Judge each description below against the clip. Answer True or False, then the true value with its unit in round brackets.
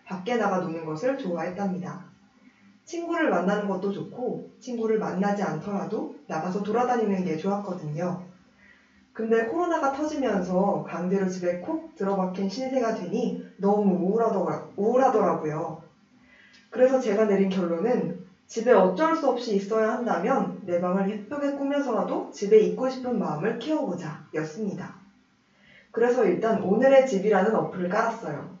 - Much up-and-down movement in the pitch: False (4.5 semitones)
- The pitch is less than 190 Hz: False (205 Hz)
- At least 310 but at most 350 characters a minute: True (320 characters per minute)